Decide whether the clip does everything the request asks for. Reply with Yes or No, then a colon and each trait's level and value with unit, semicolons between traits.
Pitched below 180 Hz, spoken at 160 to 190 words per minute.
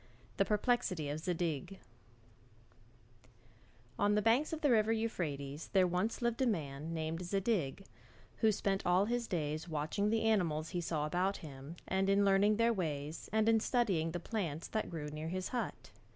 No: medium, 185 Hz; average, 165 wpm